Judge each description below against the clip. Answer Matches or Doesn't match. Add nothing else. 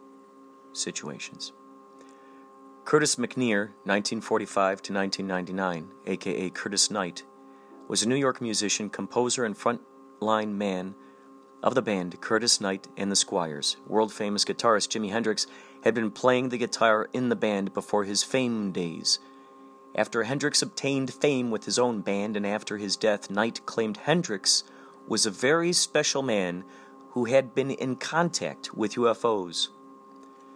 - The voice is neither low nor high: Doesn't match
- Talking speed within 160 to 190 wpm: Doesn't match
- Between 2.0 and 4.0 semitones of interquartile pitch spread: Doesn't match